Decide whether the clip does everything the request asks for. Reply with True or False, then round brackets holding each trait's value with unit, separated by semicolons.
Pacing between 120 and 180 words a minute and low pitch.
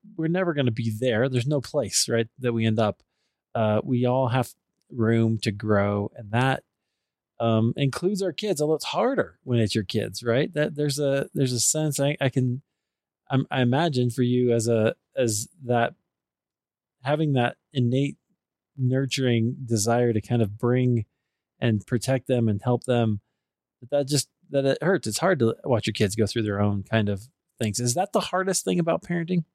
False (190 wpm; 125 Hz)